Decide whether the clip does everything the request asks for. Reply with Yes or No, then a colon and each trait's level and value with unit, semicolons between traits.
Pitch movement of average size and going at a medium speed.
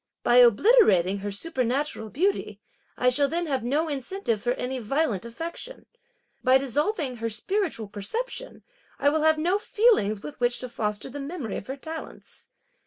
No: wide, 5.9 semitones; average, 160 wpm